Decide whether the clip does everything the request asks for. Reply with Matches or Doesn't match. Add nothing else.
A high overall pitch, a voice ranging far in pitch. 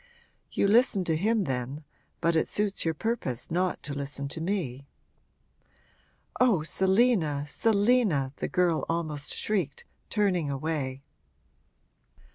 Doesn't match